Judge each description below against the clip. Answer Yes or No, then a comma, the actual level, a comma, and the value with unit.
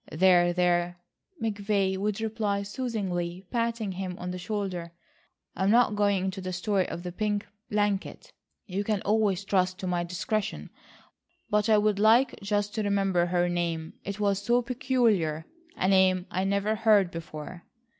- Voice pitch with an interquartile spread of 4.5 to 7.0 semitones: No, average, 2.8 semitones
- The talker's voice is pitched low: No, high, 195 Hz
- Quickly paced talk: No, average, 155 wpm